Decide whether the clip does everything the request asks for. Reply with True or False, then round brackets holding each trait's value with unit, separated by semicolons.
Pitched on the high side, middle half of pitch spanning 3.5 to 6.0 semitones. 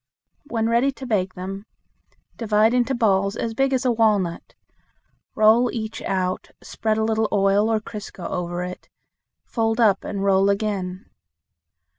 False (215 Hz; 2.7 semitones)